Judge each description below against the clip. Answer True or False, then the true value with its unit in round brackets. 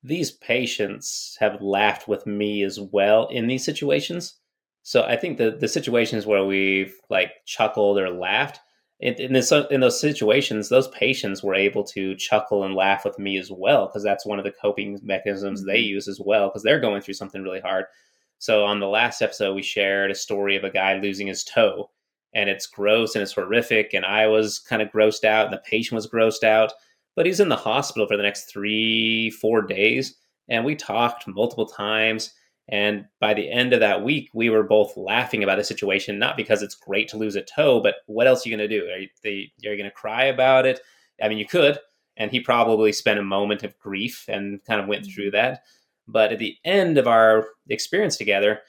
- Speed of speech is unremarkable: False (215 wpm)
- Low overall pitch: True (105 Hz)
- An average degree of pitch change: False (2.2 semitones)